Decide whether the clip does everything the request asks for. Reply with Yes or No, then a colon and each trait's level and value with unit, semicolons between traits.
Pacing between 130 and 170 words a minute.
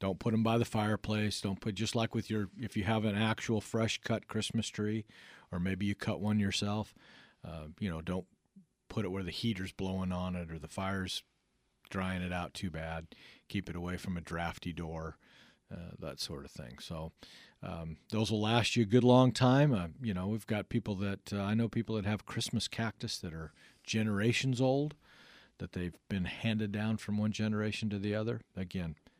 No: fast, 205 wpm